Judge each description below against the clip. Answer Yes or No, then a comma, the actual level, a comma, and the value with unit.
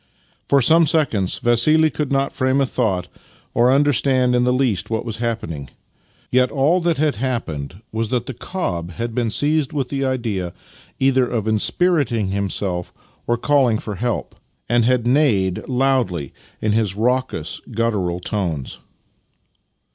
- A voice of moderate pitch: No, low, 120 Hz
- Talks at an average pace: Yes, average, 150 wpm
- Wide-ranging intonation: No, average, 4.6 semitones